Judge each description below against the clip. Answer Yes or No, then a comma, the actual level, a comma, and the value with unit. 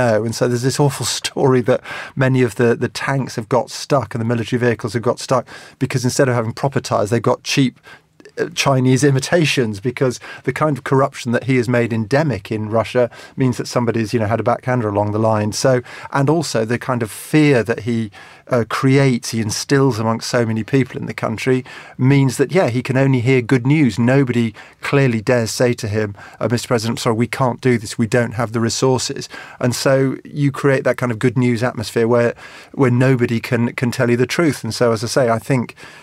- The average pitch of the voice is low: Yes, low, 125 Hz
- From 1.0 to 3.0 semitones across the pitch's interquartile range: Yes, narrow, 2.4 semitones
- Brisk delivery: Yes, fast, 215 wpm